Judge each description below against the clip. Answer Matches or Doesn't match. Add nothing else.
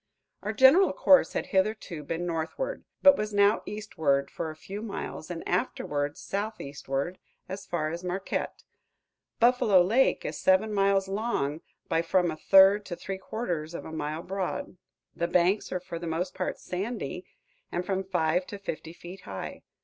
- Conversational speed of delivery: Matches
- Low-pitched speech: Doesn't match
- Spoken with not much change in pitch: Doesn't match